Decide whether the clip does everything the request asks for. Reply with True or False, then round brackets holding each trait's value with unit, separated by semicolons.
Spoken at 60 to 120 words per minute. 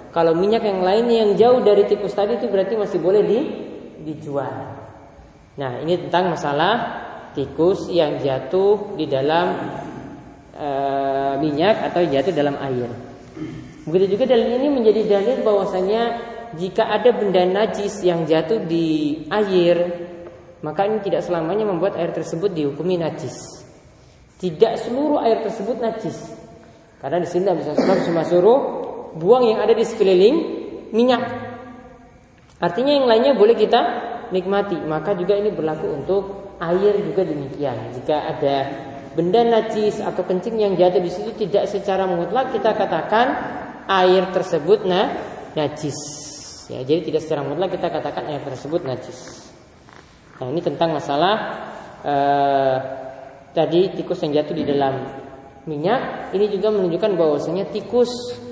False (135 wpm)